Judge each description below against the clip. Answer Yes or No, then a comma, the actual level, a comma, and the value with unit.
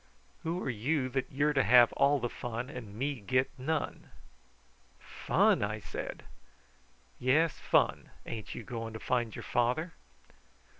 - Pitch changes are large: No, average, 3.7 semitones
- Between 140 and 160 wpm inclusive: Yes, average, 145 wpm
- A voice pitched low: Yes, low, 125 Hz